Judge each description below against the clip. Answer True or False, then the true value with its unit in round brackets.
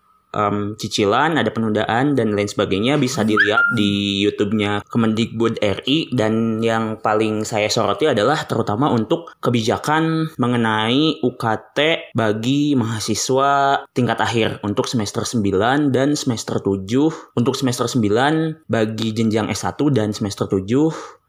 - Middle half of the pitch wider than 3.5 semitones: True (4.0 semitones)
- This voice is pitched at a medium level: False (115 Hz)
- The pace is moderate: True (120 wpm)